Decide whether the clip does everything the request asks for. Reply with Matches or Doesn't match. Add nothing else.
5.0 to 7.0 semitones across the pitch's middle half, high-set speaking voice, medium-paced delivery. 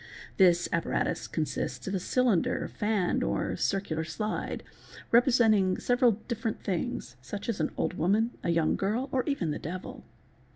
Matches